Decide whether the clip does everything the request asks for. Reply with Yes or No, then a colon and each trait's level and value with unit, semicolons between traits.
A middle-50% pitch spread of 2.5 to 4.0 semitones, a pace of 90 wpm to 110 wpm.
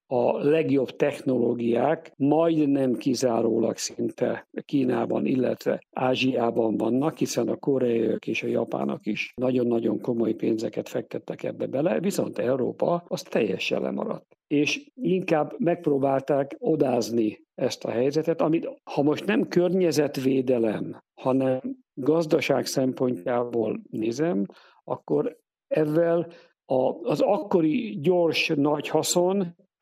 No: average, 5.1 semitones; slow, 105 wpm